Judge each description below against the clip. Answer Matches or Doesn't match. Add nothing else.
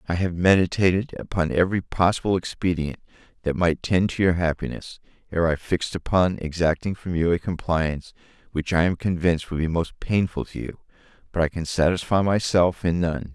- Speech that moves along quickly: Doesn't match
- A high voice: Doesn't match